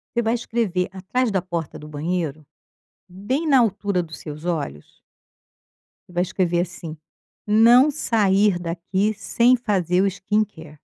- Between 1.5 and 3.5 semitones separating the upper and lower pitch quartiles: No, average, 4.2 semitones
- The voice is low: No, high, 190 Hz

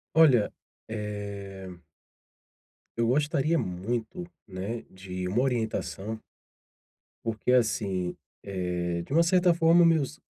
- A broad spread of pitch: Yes, wide, 6.7 semitones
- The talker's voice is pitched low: Yes, low, 110 Hz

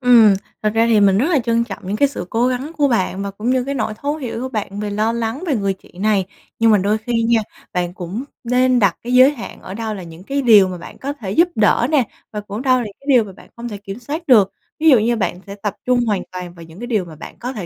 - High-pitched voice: Yes, high, 225 Hz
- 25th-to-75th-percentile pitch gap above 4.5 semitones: No, average, 4.1 semitones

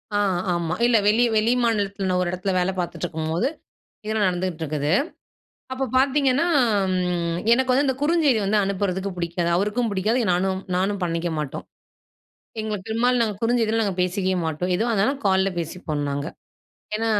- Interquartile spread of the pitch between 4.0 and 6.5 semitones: Yes, average, 4.3 semitones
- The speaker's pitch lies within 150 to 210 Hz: Yes, high, 195 Hz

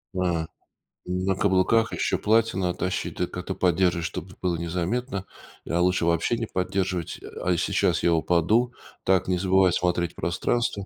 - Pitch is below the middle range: Yes, very low, 90 Hz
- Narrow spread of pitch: Yes, narrow, 1.9 semitones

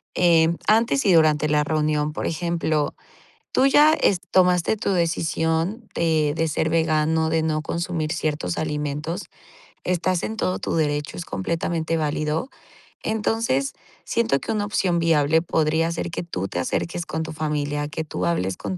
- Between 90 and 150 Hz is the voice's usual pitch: No, medium, 160 Hz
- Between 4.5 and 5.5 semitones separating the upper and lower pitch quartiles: No, narrow, 2.5 semitones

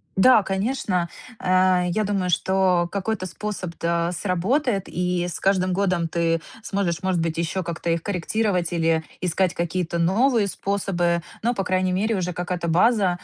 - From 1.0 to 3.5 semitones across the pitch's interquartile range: Yes, narrow, 2.4 semitones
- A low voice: No, medium, 185 Hz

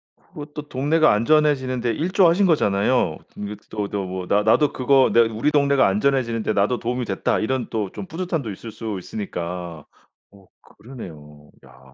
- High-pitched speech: No, low, 115 Hz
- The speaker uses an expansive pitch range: Yes, wide, 5.9 semitones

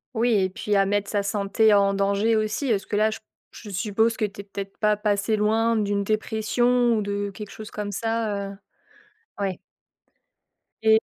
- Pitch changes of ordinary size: No, narrow, 1.6 semitones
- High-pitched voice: Yes, high, 210 Hz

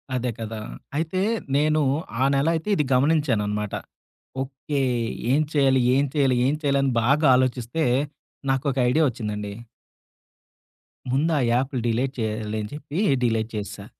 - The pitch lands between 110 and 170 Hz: Yes, low, 135 Hz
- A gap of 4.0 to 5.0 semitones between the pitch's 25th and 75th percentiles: Yes, average, 4.4 semitones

